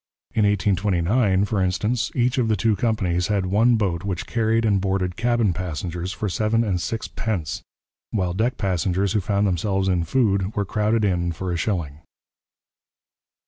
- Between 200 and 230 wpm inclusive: No, average, 165 wpm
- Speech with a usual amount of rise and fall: Yes, average, 3.4 semitones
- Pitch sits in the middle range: No, low, 100 Hz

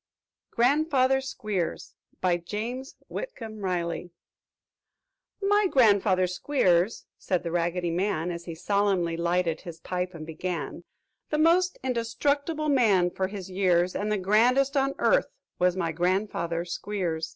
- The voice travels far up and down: Yes, wide, 6.4 semitones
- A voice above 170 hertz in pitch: Yes, high, 190 Hz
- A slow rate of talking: Yes, slow, 130 wpm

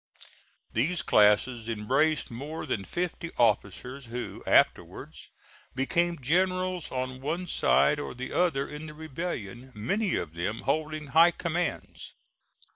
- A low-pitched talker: No, medium, 145 Hz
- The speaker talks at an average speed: No, slow, 120 wpm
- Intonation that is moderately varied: No, wide, 6.0 semitones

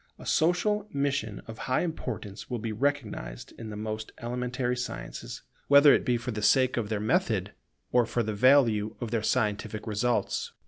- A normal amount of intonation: Yes, average, 3.7 semitones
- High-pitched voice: No, low, 120 Hz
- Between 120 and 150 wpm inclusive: No, average, 175 wpm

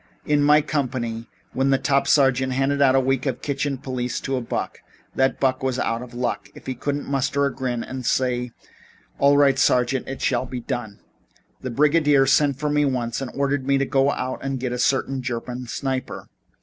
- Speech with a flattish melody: Yes, narrow, 1.8 semitones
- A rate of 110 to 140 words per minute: No, average, 200 wpm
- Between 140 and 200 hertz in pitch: No, low, 130 Hz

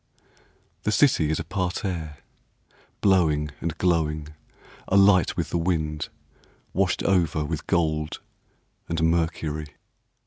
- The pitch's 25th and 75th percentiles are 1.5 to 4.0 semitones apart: Yes, average, 3.1 semitones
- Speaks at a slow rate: Yes, slow, 110 wpm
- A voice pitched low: Yes, very low, 80 Hz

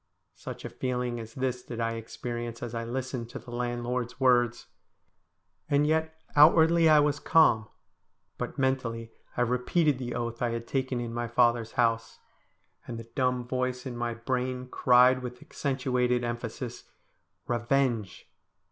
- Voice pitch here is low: Yes, low, 125 Hz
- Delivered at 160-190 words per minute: No, average, 150 wpm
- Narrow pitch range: Yes, narrow, 1.7 semitones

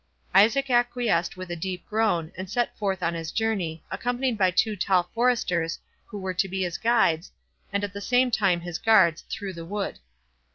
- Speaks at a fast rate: No, average, 190 wpm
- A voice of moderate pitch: No, high, 195 Hz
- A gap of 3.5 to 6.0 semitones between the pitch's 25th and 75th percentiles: Yes, average, 4.2 semitones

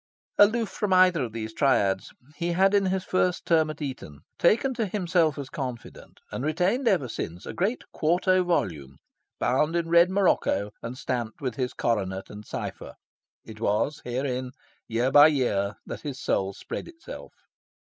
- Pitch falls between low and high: Yes, medium, 145 Hz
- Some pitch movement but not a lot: No, wide, 7.9 semitones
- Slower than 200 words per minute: Yes, average, 165 wpm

